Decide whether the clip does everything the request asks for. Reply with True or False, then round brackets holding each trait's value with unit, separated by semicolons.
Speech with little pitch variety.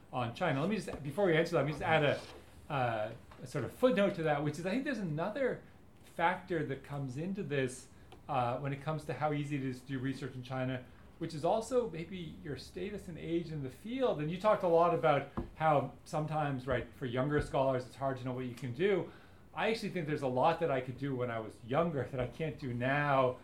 False (4.6 semitones)